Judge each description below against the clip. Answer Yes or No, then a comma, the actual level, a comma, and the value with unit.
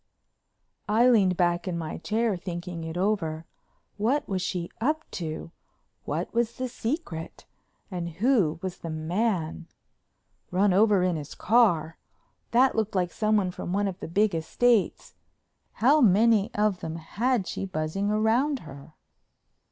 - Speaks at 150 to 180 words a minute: No, average, 140 wpm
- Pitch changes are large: No, average, 4.8 semitones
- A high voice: Yes, high, 195 Hz